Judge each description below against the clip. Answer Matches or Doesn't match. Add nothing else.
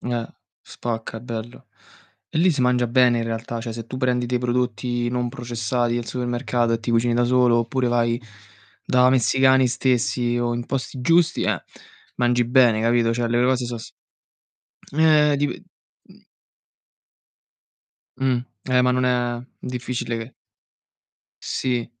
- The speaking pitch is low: Matches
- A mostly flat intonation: Matches